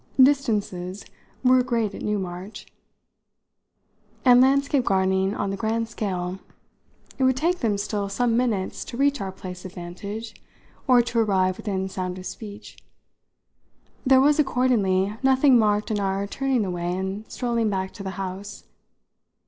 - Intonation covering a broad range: No, average, 4.5 semitones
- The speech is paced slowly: No, average, 145 wpm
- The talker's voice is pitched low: No, high, 210 Hz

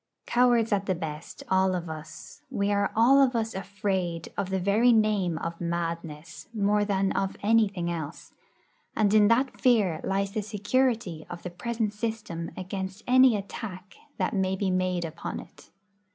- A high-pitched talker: Yes, high, 195 Hz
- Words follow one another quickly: No, average, 165 wpm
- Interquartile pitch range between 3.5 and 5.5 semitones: Yes, average, 3.8 semitones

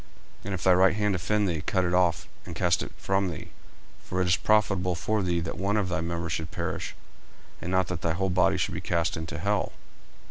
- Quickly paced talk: Yes, fast, 235 wpm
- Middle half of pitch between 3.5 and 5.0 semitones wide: No, narrow, 2.4 semitones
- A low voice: Yes, very low, 90 Hz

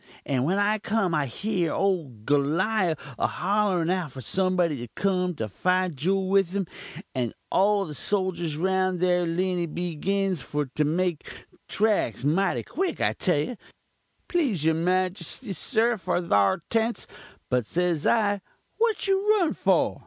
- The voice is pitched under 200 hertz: Yes, medium, 185 Hz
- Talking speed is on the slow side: No, average, 155 wpm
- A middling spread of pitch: Yes, average, 3.9 semitones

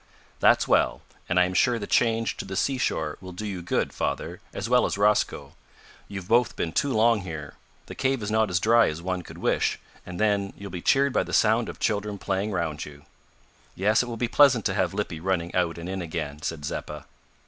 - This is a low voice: Yes, very low, 95 Hz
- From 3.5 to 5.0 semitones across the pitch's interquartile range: Yes, average, 4.5 semitones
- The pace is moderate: No, fast, 220 wpm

